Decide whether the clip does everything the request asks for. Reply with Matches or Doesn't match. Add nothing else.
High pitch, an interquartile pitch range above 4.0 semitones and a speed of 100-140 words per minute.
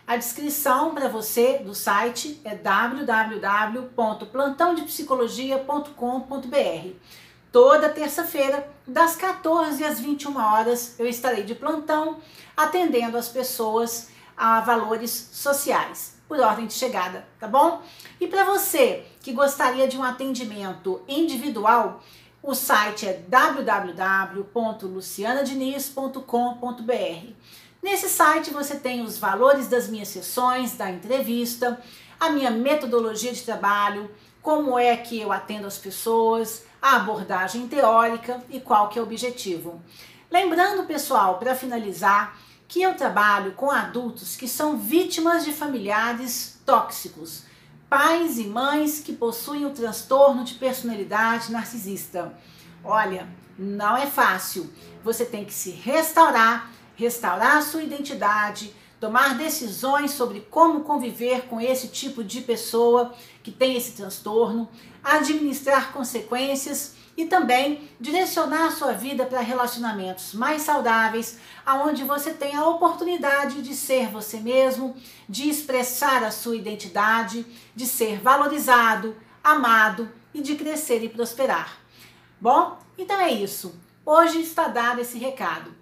Matches